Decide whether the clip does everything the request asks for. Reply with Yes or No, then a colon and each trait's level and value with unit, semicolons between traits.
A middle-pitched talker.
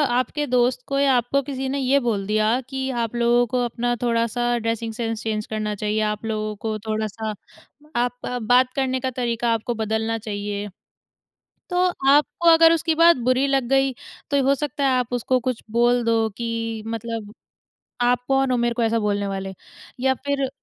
No: high, 240 Hz